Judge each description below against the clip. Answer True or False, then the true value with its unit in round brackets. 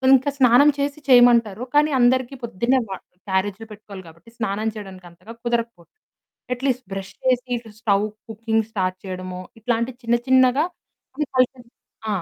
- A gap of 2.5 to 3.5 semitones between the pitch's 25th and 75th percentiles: False (4.2 semitones)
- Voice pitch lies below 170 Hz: False (230 Hz)